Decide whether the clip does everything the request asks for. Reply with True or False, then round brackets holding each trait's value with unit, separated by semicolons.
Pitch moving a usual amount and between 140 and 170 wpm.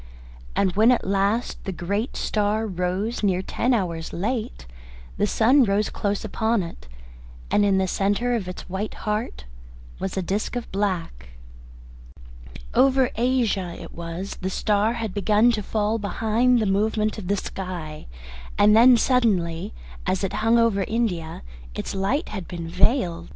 True (3.3 semitones; 155 wpm)